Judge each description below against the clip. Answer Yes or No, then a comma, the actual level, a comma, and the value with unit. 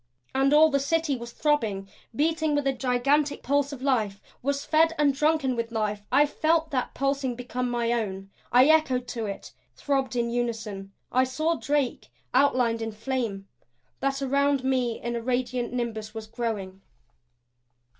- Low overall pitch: No, very high, 255 Hz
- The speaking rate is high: No, average, 155 wpm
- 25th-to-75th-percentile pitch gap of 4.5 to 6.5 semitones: No, average, 3.5 semitones